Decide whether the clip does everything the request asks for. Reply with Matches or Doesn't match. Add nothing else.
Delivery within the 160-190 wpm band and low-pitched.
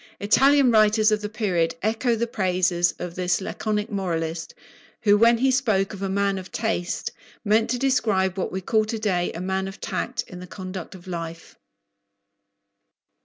Doesn't match